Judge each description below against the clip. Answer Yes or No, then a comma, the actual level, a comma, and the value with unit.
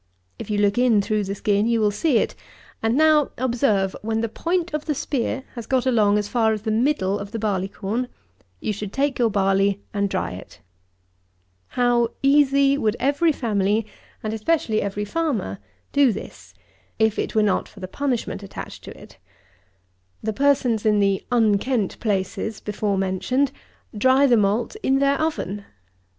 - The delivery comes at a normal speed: Yes, average, 170 wpm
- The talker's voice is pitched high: Yes, high, 220 Hz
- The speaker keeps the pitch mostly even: No, average, 4.6 semitones